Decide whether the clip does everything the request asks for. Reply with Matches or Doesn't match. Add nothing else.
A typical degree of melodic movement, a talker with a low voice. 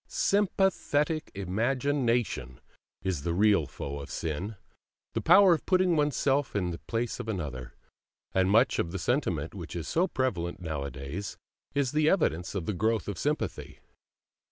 Doesn't match